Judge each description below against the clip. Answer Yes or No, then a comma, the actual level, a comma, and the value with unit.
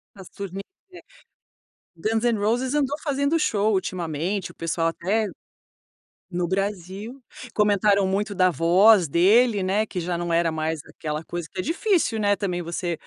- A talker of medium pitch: No, high, 195 Hz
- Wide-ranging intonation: No, average, 4.0 semitones